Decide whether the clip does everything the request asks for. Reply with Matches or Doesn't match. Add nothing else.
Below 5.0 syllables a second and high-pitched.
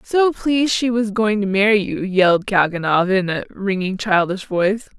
Matches